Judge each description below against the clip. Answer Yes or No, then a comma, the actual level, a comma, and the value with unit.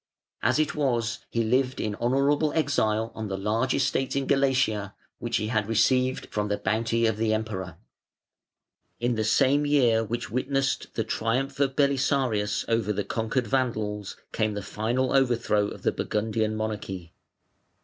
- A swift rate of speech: No, average, 160 wpm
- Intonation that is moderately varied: Yes, average, 3.6 semitones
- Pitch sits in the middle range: No, low, 115 Hz